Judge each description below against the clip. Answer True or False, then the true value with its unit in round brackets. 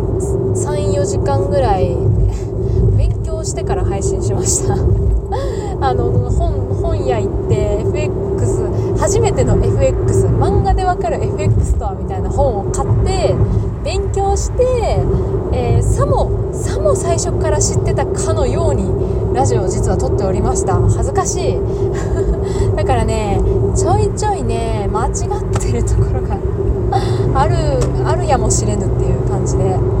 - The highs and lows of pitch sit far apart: False (4.4 semitones)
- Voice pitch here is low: True (120 Hz)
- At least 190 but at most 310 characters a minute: True (255 characters per minute)